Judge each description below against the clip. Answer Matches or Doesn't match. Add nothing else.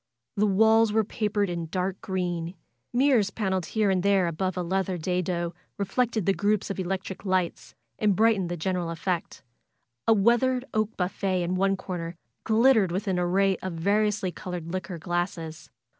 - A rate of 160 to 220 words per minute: Matches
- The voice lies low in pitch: Doesn't match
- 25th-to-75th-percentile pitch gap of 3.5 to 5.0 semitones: Doesn't match